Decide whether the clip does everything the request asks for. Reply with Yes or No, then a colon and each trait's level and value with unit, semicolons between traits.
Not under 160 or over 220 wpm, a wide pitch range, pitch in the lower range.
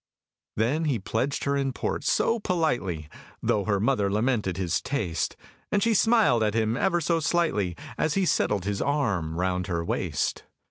Yes: average, 170 wpm; wide, 8.1 semitones; low, 115 Hz